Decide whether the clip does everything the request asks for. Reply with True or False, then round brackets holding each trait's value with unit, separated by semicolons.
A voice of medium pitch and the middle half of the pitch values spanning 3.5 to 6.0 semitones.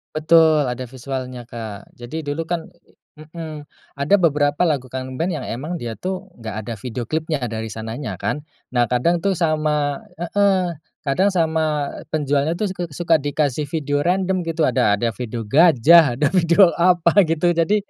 True (155 Hz; 4.7 semitones)